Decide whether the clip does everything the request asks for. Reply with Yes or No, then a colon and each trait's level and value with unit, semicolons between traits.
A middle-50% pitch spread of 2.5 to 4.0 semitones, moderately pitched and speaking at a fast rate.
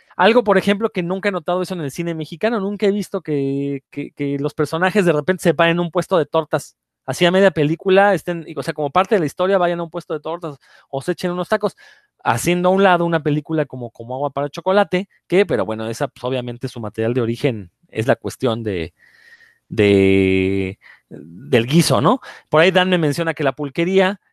No: average, 4.8 semitones; medium, 170 Hz; fast, 220 wpm